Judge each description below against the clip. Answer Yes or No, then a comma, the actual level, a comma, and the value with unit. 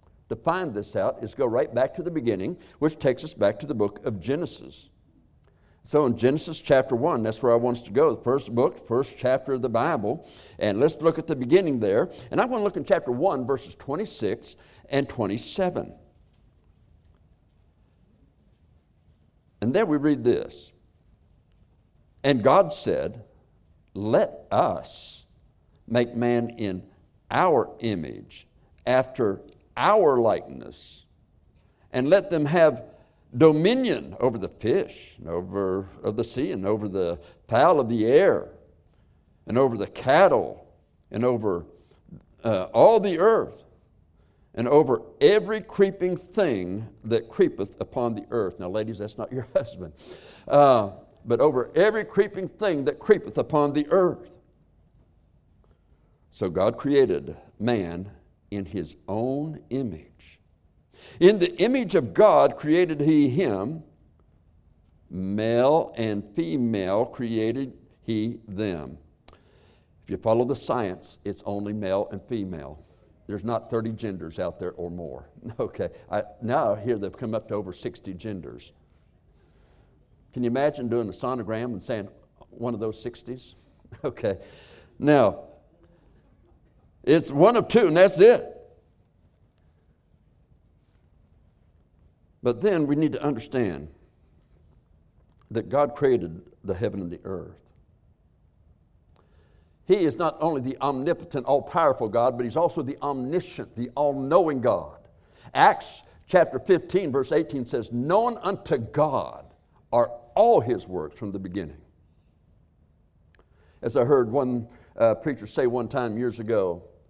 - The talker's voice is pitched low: Yes, low, 115 Hz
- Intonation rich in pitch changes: Yes, wide, 8.0 semitones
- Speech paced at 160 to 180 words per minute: No, slow, 135 wpm